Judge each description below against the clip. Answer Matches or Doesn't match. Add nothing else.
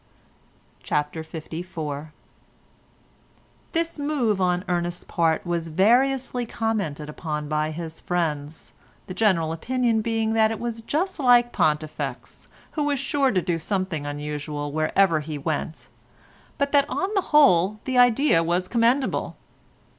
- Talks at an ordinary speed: Doesn't match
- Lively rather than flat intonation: Matches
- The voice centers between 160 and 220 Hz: Matches